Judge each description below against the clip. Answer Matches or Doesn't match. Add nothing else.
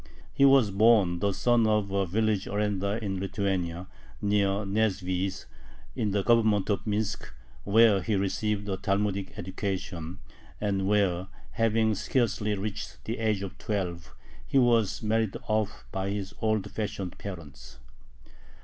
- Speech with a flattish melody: Matches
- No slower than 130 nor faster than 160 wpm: Matches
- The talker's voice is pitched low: Matches